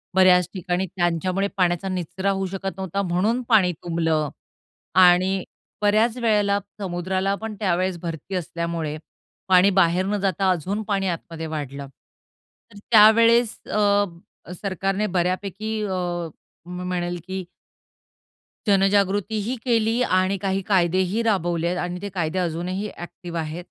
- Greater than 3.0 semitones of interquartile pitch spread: No, narrow, 2.4 semitones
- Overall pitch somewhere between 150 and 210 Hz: Yes, medium, 185 Hz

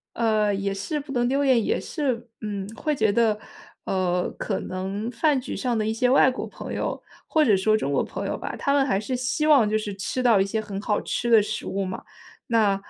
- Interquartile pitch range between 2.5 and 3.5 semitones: No, average, 4.4 semitones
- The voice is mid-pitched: No, high, 220 Hz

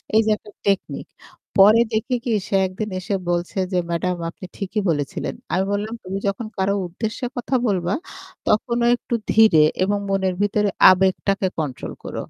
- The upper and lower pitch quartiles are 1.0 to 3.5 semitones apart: Yes, average, 2.7 semitones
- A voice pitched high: Yes, high, 195 Hz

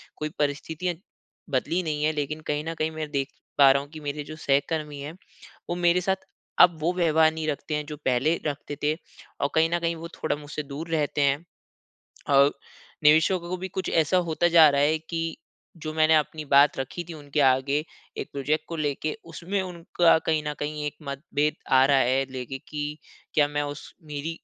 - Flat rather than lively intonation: Yes, narrow, 2.1 semitones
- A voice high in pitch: No, medium, 150 Hz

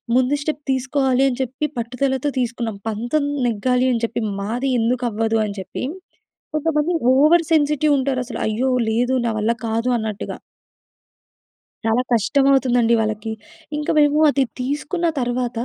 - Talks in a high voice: Yes, very high, 250 Hz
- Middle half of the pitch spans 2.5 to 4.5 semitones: Yes, average, 3.5 semitones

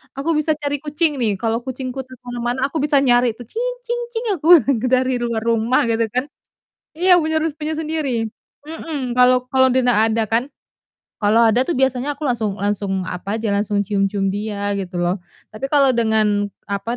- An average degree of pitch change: Yes, average, 4.9 semitones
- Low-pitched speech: No, high, 245 Hz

